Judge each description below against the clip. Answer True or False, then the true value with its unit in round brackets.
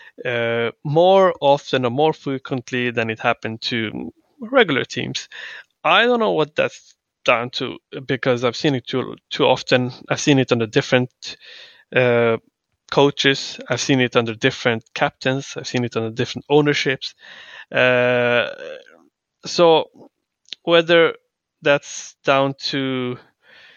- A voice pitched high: False (135 Hz)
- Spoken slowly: True (130 wpm)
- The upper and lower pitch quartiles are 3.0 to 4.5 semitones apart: True (3.8 semitones)